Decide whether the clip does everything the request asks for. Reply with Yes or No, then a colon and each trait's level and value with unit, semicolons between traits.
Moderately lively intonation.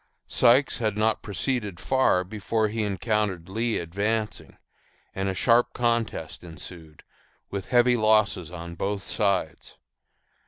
Yes: average, 3.6 semitones